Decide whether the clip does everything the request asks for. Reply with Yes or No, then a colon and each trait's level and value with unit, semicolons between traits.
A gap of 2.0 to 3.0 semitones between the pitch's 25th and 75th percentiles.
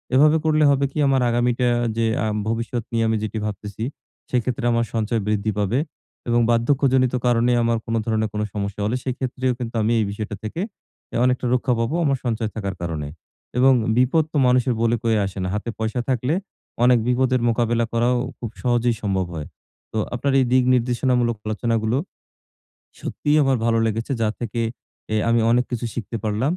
Yes: narrow, 2.4 semitones